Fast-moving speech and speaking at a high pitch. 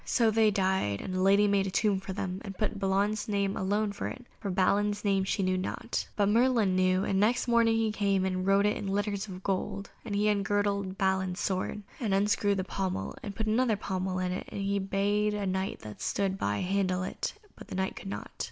Yes: fast, 220 wpm; high, 195 Hz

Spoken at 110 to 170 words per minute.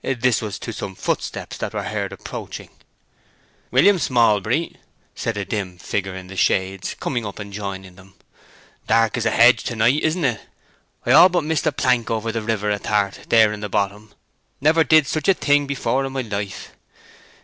No: average, 180 wpm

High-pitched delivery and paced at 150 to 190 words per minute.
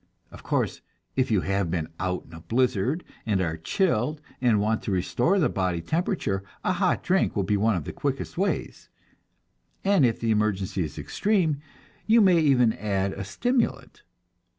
No: low, 110 Hz; average, 175 wpm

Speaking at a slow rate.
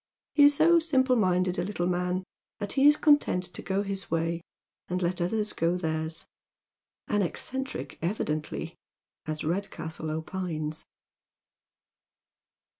Yes: slow, 130 wpm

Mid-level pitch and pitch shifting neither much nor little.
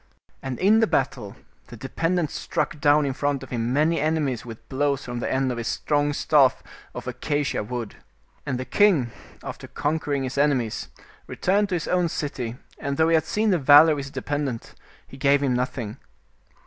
Yes: medium, 145 Hz; average, 3.4 semitones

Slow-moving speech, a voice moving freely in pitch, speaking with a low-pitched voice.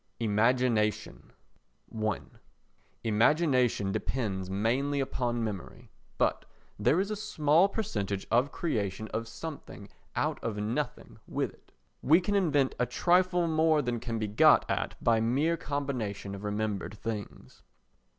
Yes: slow, 130 wpm; wide, 5.9 semitones; low, 120 Hz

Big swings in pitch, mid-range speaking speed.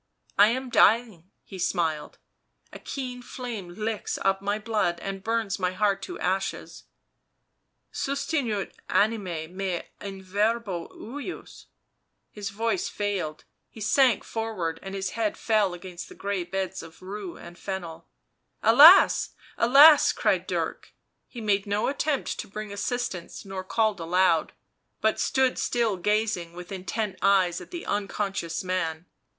No: average, 3.6 semitones; average, 150 wpm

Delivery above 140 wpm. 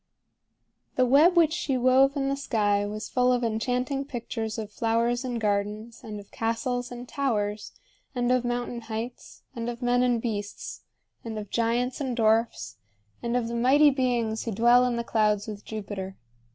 Yes: average, 175 wpm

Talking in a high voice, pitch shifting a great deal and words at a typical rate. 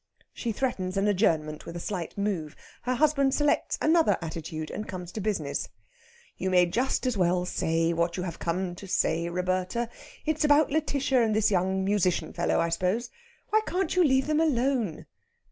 Yes: high, 195 Hz; wide, 7.2 semitones; average, 180 wpm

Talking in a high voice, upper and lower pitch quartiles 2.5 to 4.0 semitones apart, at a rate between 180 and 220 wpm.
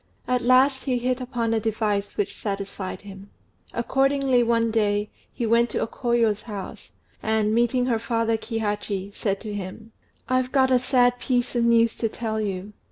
No: high, 230 Hz; average, 3.0 semitones; average, 170 wpm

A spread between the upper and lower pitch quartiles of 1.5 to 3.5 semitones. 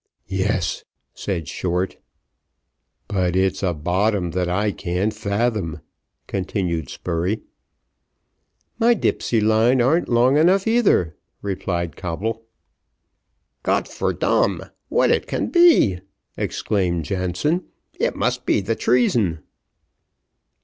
No: average, 4.8 semitones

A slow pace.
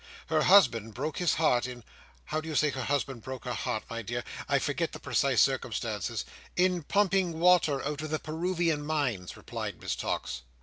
No: average, 180 wpm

